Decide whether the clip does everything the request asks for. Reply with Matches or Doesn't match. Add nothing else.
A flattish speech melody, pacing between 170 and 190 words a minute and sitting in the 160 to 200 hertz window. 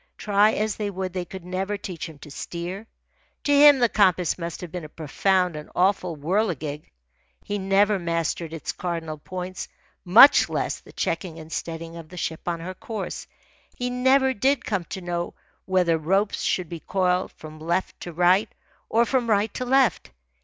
Doesn't match